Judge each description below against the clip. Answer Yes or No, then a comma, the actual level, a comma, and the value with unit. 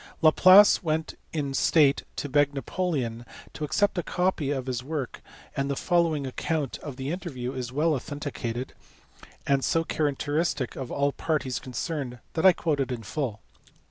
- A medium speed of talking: Yes, average, 165 wpm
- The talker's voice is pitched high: No, medium, 145 Hz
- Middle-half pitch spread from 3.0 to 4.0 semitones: Yes, average, 3.5 semitones